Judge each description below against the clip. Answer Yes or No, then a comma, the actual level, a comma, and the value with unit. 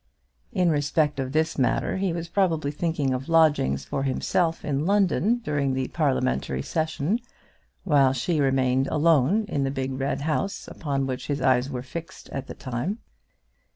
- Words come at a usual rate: Yes, average, 160 wpm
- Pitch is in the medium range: Yes, medium, 145 Hz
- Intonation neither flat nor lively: Yes, average, 3.9 semitones